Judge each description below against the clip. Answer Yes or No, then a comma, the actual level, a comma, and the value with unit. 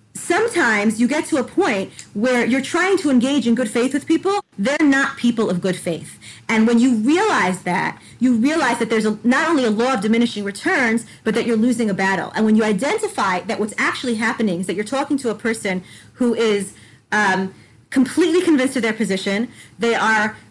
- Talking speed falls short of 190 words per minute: No, fast, 205 wpm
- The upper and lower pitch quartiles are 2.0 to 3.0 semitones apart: No, average, 4.2 semitones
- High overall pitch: Yes, high, 235 Hz